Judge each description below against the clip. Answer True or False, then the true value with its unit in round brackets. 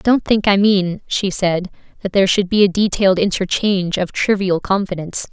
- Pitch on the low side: False (190 Hz)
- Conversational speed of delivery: True (180 wpm)